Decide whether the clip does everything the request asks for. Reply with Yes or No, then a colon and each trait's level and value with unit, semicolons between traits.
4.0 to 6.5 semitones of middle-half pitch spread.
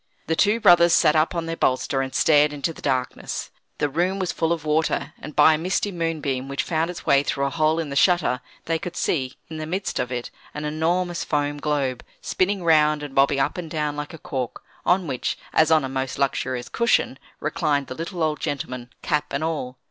No: average, 3.2 semitones